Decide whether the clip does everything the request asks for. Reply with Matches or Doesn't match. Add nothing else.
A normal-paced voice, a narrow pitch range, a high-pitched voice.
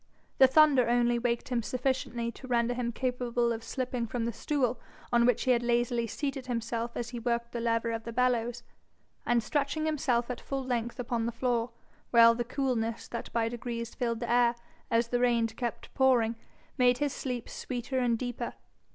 Matches